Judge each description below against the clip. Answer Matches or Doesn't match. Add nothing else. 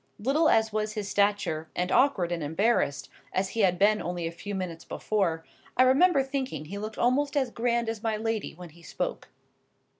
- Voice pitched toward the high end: Matches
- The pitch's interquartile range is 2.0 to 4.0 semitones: Doesn't match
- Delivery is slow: Doesn't match